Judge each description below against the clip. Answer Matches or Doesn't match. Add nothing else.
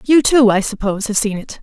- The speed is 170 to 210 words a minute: Doesn't match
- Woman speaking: Matches